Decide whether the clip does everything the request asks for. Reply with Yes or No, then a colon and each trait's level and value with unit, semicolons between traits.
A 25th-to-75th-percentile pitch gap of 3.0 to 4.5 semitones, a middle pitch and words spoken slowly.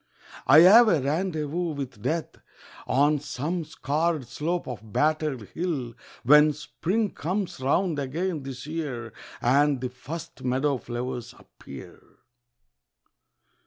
Yes: average, 4.2 semitones; medium, 150 Hz; slow, 115 wpm